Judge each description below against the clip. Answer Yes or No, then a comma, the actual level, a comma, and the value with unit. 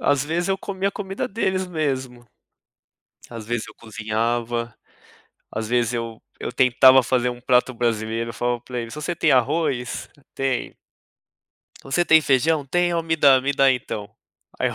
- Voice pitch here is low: Yes, low, 130 Hz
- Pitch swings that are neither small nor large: Yes, average, 5.0 semitones